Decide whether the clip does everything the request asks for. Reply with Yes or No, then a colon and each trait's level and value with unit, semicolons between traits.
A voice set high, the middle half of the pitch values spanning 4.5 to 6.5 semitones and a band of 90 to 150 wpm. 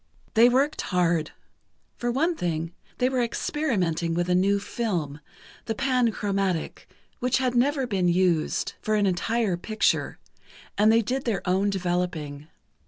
Yes: high, 200 Hz; wide, 5.5 semitones; average, 140 wpm